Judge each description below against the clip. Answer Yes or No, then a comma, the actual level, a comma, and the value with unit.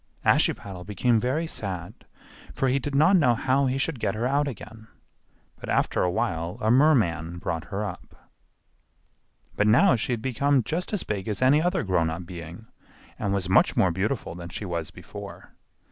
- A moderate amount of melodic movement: No, wide, 6.8 semitones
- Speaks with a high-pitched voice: No, low, 110 Hz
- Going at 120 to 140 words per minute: No, average, 180 wpm